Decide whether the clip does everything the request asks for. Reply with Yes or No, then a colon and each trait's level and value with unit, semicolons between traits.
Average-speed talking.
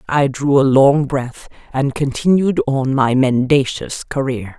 Yes: average, 145 wpm